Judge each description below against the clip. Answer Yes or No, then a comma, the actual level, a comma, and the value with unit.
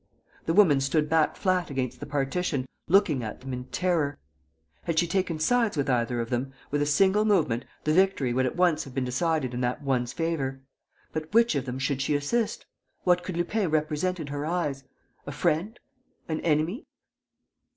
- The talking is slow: No, average, 185 wpm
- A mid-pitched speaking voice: Yes, medium, 150 Hz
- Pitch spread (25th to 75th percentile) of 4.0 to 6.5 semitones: Yes, average, 4.9 semitones